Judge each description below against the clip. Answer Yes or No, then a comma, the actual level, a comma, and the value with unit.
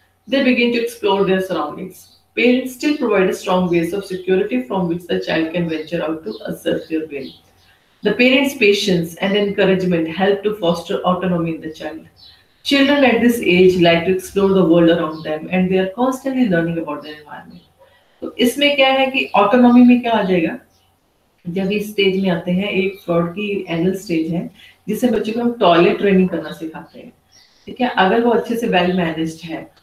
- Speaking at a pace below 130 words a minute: No, fast, 190 wpm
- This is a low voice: No, high, 190 Hz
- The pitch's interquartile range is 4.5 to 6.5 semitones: Yes, average, 4.9 semitones